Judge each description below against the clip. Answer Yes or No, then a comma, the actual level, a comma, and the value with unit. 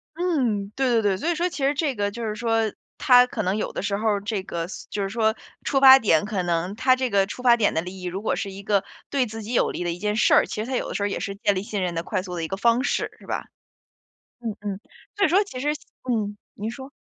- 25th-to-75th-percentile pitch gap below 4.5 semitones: Yes, average, 4.1 semitones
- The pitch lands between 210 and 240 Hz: Yes, high, 215 Hz